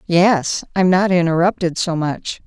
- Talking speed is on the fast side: No, average, 145 wpm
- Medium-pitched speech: Yes, medium, 175 Hz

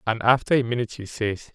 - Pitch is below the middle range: Yes, low, 115 Hz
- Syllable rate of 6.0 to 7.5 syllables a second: Yes, 6.3 syllables/s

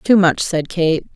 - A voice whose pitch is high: No, medium, 175 Hz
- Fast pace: Yes, fast, 210 wpm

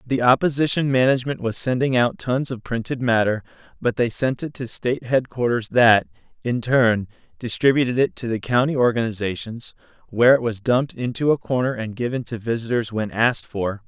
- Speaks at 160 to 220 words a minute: Yes, average, 175 wpm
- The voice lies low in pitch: Yes, low, 120 Hz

